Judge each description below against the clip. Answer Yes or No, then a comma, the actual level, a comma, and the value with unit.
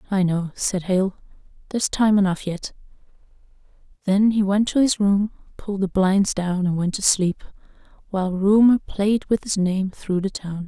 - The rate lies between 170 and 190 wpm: Yes, average, 175 wpm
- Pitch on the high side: Yes, high, 195 Hz